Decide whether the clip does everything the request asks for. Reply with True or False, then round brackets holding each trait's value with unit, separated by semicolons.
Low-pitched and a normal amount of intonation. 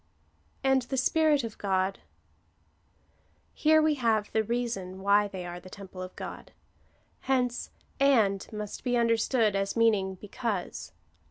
False (220 Hz; 4.1 semitones)